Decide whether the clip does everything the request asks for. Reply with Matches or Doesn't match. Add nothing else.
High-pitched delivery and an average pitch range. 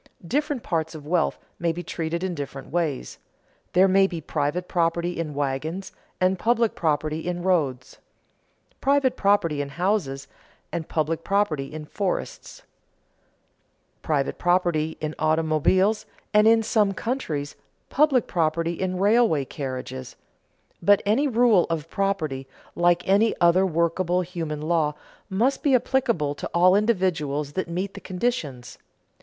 Doesn't match